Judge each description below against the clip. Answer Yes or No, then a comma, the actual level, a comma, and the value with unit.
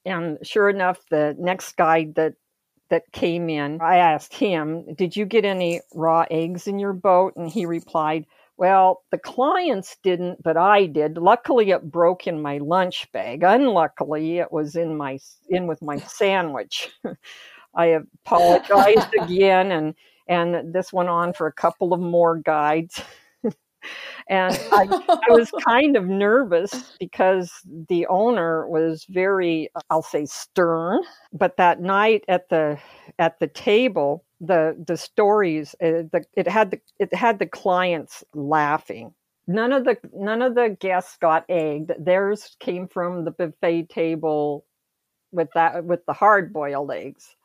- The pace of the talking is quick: No, average, 150 wpm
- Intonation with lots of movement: No, average, 3.2 semitones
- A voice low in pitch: No, medium, 175 Hz